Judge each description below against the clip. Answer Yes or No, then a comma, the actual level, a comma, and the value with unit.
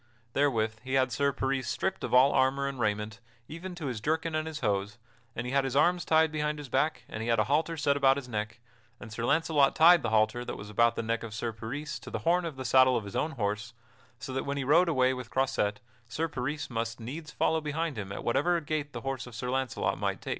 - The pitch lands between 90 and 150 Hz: Yes, low, 135 Hz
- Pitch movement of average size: Yes, average, 4.6 semitones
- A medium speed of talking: No, fast, 250 wpm